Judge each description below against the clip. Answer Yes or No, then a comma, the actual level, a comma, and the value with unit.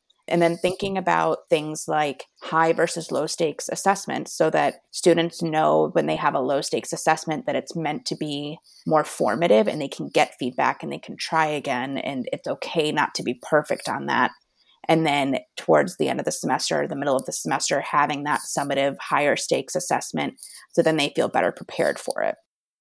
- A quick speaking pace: No, average, 195 wpm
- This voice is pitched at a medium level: Yes, medium, 160 Hz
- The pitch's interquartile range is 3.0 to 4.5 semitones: No, narrow, 2.4 semitones